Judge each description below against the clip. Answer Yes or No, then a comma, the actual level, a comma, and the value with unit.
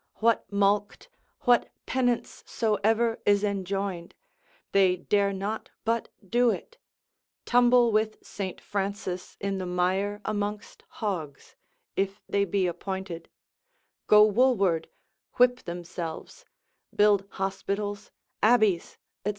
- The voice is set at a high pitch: Yes, high, 200 Hz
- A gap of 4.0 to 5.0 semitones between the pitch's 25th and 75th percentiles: No, narrow, 2.4 semitones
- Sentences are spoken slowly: Yes, slow, 105 wpm